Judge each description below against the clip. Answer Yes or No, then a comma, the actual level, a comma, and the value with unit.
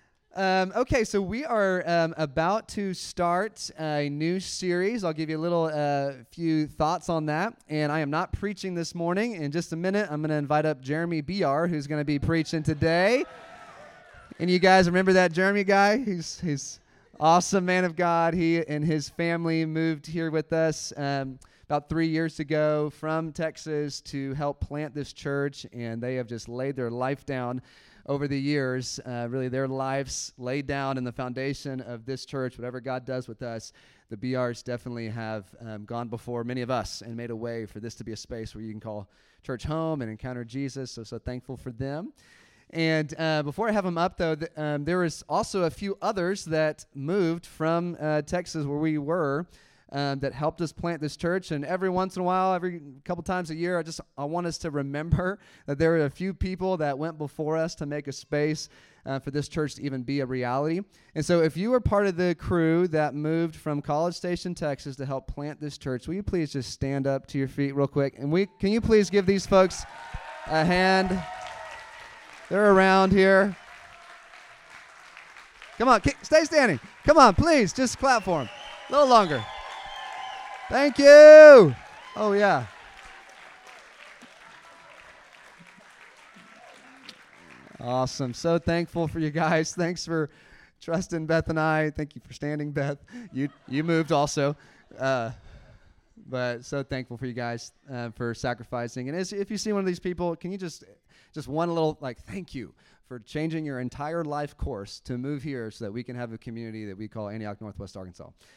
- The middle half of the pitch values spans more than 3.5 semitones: Yes, average, 4.7 semitones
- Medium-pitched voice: Yes, medium, 155 Hz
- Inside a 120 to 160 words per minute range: No, average, 190 wpm